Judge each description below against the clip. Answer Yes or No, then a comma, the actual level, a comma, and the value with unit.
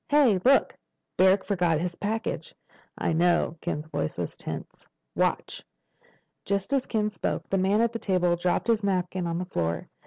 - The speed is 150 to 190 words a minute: Yes, average, 160 wpm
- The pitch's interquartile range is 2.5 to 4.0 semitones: Yes, average, 3.5 semitones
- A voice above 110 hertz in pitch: Yes, medium, 185 Hz